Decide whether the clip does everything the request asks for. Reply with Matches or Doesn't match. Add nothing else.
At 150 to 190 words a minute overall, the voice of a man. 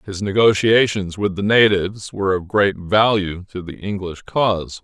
Matches